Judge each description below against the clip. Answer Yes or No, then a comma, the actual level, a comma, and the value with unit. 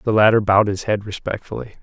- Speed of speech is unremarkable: Yes, average, 195 wpm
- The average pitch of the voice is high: No, low, 105 Hz